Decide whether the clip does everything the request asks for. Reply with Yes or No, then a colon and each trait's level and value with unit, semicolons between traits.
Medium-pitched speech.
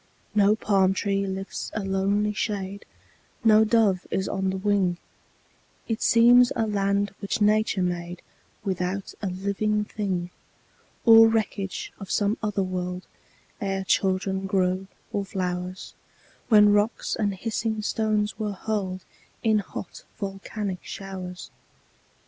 No: high, 200 Hz